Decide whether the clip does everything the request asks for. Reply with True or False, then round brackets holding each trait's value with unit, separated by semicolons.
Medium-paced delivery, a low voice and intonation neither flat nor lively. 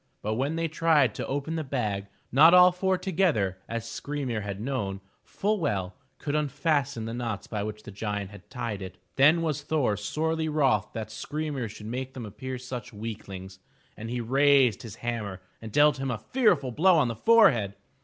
False (185 wpm; 125 Hz; 6.1 semitones)